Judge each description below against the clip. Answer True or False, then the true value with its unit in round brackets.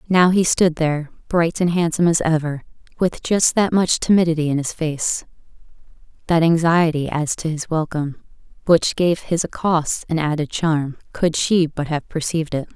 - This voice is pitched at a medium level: True (165 Hz)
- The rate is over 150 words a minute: True (170 wpm)